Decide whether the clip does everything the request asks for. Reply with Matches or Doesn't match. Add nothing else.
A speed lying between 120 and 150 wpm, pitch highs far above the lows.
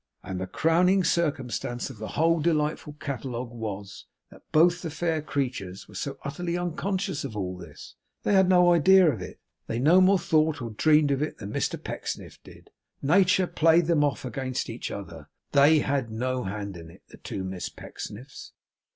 Doesn't match